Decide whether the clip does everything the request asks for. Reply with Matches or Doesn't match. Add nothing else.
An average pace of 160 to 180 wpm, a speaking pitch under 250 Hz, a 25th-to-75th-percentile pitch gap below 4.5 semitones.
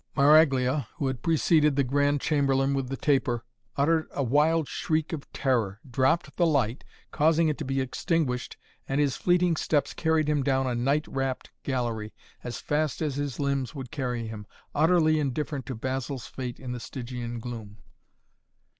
Matches